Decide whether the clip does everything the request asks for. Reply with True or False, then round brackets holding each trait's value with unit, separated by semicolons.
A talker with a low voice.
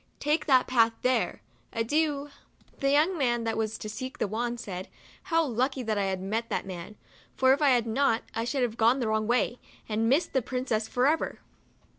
False (240 Hz)